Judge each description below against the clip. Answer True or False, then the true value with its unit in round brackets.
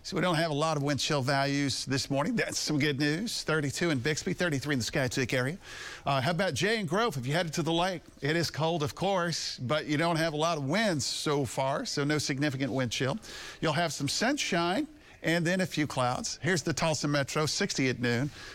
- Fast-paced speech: True (235 wpm)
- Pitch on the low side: False (150 Hz)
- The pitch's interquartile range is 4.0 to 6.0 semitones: False (3.6 semitones)